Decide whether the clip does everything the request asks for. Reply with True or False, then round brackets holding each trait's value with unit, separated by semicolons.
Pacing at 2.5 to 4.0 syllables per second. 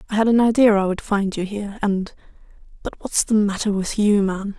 False (5.4 syllables/s)